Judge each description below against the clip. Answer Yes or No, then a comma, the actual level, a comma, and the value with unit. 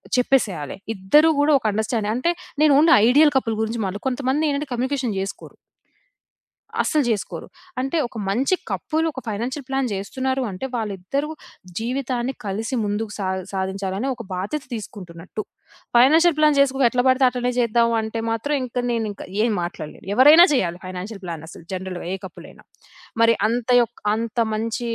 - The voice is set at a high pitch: Yes, high, 235 Hz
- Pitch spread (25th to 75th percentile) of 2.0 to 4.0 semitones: No, average, 4.8 semitones